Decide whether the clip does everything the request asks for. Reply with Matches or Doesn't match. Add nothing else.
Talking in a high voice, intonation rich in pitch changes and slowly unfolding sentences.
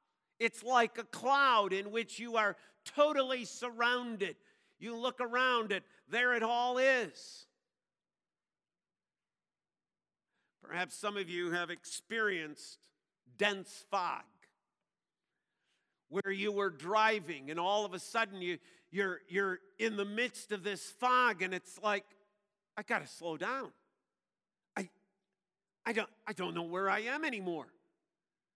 Doesn't match